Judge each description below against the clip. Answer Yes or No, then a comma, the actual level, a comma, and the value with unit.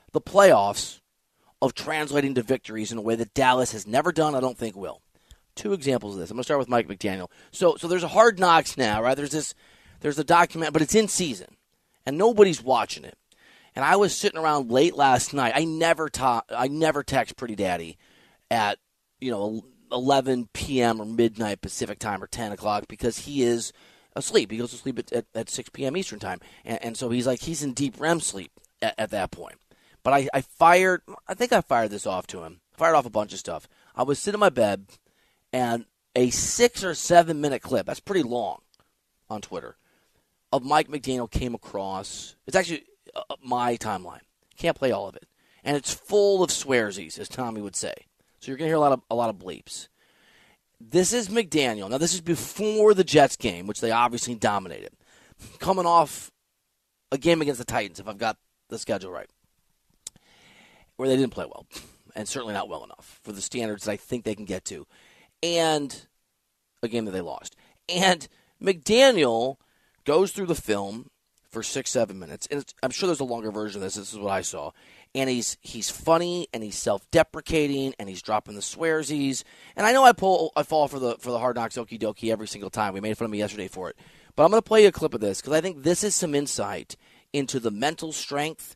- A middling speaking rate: No, fast, 210 wpm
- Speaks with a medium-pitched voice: No, low, 130 Hz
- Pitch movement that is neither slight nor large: No, wide, 6.4 semitones